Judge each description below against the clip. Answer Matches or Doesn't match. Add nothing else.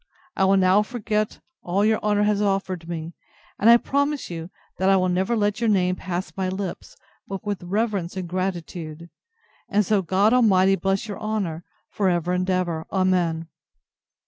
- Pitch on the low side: Doesn't match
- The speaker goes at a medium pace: Matches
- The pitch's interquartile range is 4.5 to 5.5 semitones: Doesn't match